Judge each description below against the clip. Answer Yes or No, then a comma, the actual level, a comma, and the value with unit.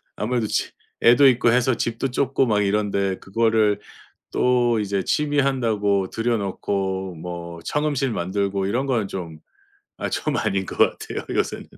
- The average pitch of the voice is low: Yes, low, 105 Hz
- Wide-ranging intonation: No, average, 4.2 semitones